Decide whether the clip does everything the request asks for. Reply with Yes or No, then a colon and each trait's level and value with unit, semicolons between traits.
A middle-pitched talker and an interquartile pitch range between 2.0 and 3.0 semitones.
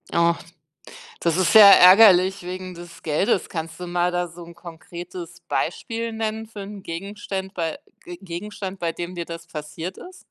Yes: medium, 180 Hz; narrow, 2.6 semitones